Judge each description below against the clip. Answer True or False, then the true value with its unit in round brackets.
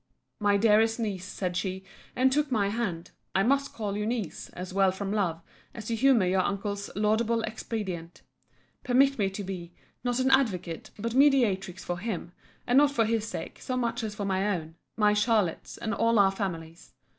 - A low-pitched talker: False (210 Hz)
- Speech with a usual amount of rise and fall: True (3.6 semitones)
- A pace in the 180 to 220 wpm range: True (190 wpm)